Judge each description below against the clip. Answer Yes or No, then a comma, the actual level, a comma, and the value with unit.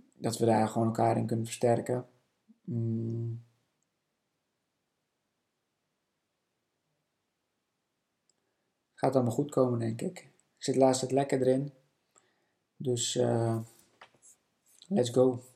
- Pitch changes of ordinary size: No, narrow, 2.1 semitones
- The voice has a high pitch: No, low, 120 Hz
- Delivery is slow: Yes, slow, 95 wpm